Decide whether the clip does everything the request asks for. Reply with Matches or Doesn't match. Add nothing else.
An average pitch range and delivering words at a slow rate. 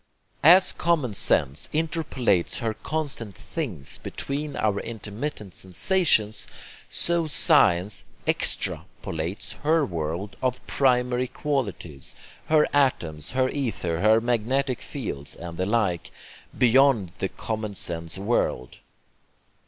Doesn't match